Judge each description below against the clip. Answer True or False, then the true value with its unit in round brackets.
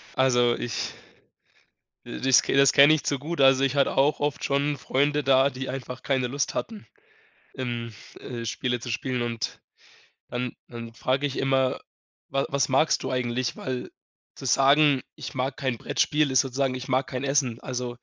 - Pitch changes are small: True (1.9 semitones)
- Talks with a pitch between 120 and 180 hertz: True (130 Hz)